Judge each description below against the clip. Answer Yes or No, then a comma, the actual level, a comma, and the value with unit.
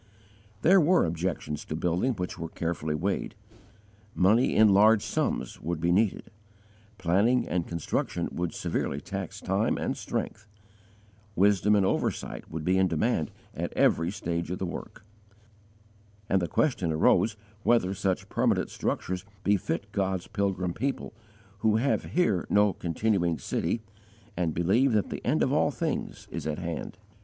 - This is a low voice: Yes, very low, 95 Hz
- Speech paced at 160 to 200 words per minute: No, average, 150 wpm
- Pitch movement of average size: Yes, average, 3.7 semitones